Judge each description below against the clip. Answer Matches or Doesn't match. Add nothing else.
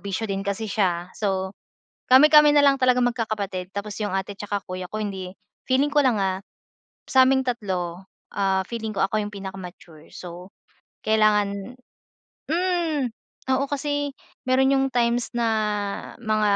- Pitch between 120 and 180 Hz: Doesn't match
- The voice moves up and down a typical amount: Matches